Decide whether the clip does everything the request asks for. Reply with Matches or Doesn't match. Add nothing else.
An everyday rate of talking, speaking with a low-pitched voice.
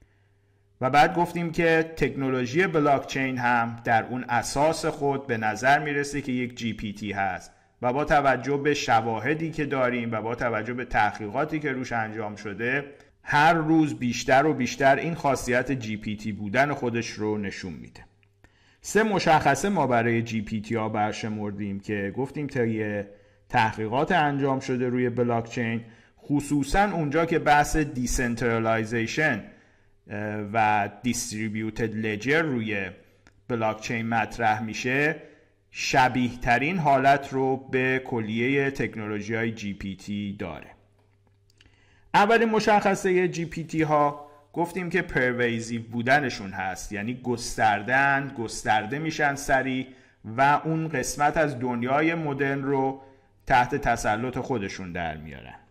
Matches